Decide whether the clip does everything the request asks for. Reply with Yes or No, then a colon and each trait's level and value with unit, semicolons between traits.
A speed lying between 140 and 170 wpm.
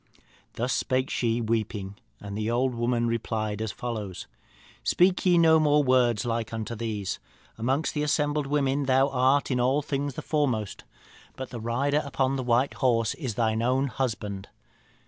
Yes: average, 165 wpm